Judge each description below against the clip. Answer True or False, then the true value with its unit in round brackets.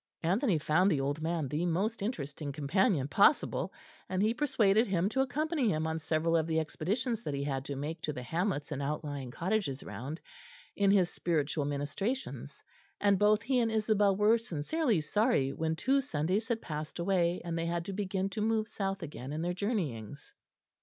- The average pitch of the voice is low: False (175 Hz)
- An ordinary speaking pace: True (185 wpm)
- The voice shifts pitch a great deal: True (5.9 semitones)